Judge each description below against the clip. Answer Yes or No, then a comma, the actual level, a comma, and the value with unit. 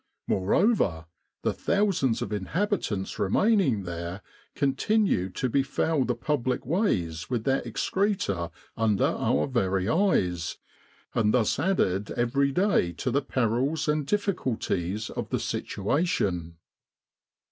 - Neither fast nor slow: No, slow, 115 wpm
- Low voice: Yes, low, 125 Hz